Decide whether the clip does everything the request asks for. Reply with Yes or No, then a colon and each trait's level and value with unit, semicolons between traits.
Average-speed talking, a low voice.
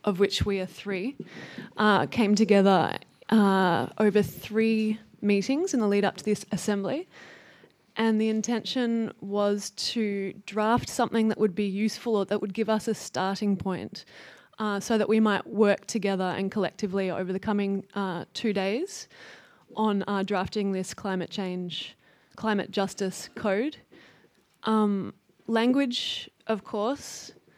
No: average, 145 wpm; high, 210 Hz